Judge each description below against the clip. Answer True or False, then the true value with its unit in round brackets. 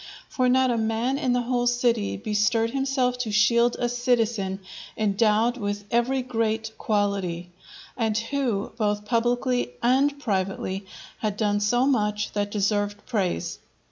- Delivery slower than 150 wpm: True (140 wpm)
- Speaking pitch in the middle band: False (225 Hz)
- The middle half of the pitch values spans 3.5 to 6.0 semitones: False (3.1 semitones)